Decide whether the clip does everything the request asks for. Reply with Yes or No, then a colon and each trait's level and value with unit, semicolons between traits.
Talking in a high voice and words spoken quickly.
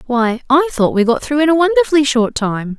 Yes: very high, 265 Hz; fast, 235 wpm